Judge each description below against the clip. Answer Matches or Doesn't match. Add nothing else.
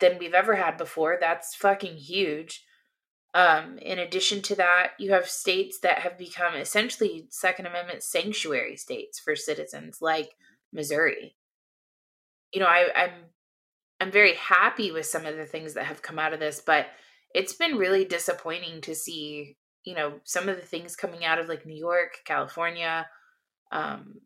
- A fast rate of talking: Doesn't match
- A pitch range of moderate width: Matches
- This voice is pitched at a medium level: Matches